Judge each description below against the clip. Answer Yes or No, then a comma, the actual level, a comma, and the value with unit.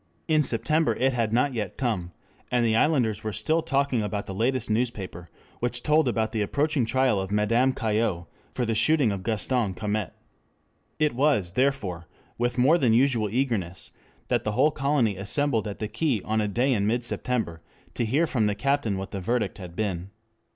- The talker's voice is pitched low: Yes, low, 115 Hz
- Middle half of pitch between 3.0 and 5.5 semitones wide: Yes, average, 4.3 semitones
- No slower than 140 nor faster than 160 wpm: No, average, 185 wpm